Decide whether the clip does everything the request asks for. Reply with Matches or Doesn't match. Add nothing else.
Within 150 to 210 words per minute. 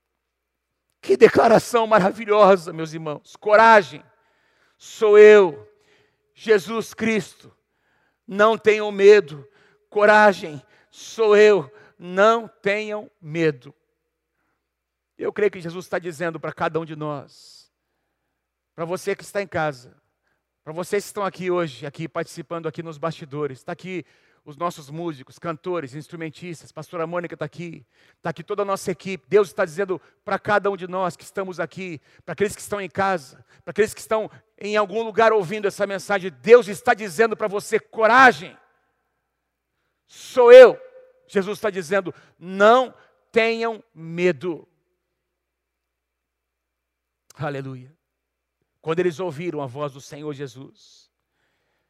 Doesn't match